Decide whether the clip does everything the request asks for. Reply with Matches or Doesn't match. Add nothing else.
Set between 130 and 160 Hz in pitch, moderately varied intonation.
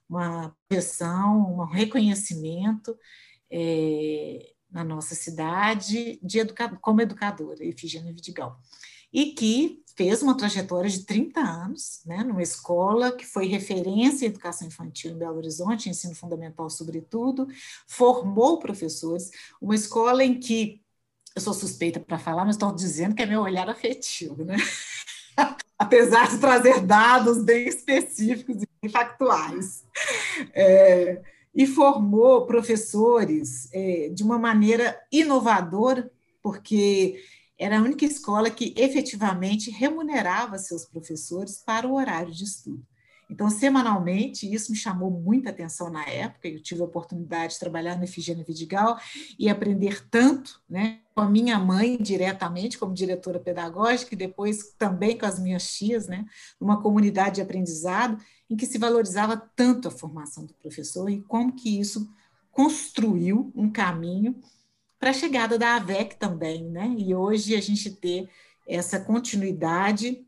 Doesn't match